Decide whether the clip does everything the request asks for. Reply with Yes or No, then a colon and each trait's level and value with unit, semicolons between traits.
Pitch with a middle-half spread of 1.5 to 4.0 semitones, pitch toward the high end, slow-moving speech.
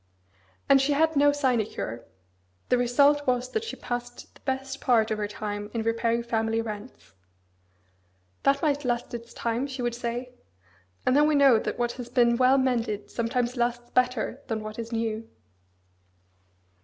No: narrow, 2.6 semitones; high, 240 Hz; average, 165 wpm